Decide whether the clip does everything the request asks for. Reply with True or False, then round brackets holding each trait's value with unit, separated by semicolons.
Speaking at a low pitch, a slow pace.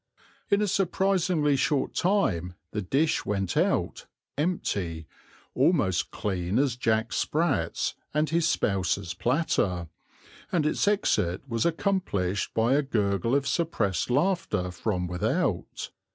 True (125 Hz; 120 wpm)